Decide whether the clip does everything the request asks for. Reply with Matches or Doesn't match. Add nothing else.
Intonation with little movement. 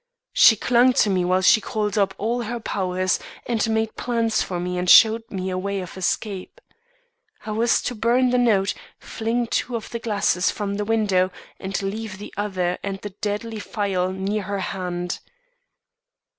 Doesn't match